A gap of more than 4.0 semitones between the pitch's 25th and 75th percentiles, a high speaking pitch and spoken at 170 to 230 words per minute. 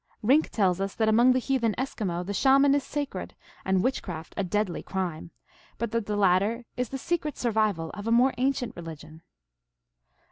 Yes: wide, 5.4 semitones; high, 215 Hz; average, 175 wpm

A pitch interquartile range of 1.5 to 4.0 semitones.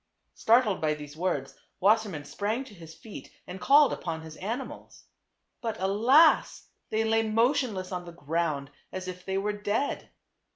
No: average, 4.8 semitones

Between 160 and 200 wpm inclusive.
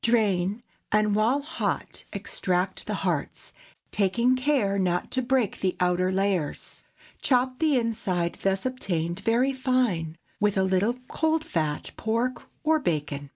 No: slow, 135 wpm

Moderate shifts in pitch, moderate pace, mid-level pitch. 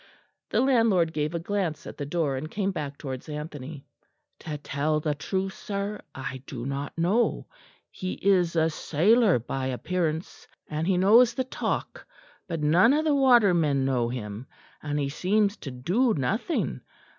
No: wide, 5.9 semitones; average, 160 wpm; medium, 160 Hz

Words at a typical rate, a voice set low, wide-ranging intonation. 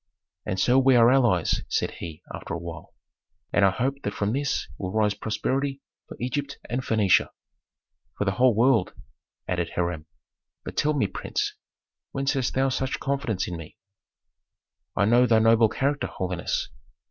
Yes: average, 160 wpm; low, 115 Hz; wide, 6.1 semitones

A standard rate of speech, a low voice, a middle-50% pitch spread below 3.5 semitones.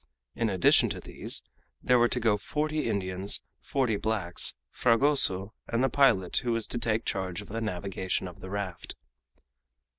No: average, 160 wpm; low, 110 Hz; average, 4.0 semitones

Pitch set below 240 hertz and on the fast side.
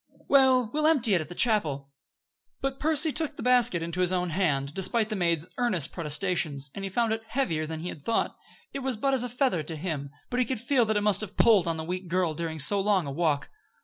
Yes: high, 190 Hz; fast, 245 wpm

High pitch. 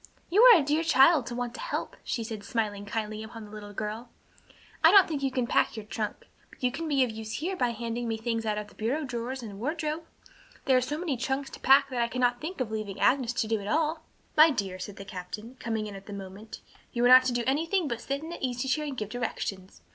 Yes: high, 240 Hz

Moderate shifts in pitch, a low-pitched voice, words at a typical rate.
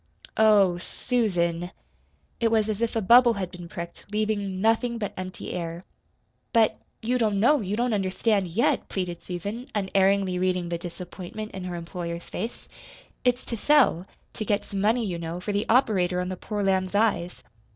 No: average, 3.7 semitones; high, 195 Hz; average, 170 wpm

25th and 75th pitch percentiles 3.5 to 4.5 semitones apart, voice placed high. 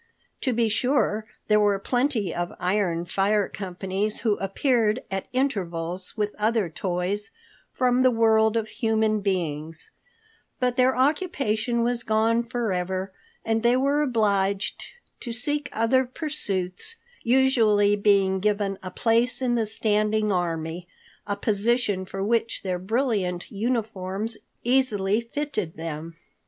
Yes: average, 3.8 semitones; high, 215 Hz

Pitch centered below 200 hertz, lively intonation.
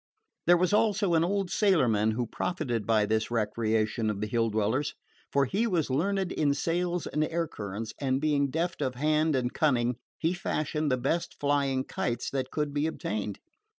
Yes: medium, 140 Hz; wide, 6.2 semitones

